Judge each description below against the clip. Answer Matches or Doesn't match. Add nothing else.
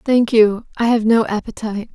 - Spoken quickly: Doesn't match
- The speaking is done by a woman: Matches